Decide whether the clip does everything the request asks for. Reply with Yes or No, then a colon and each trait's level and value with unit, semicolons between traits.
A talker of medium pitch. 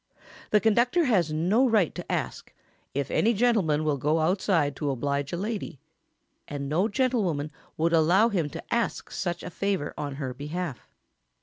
Yes: medium, 170 Hz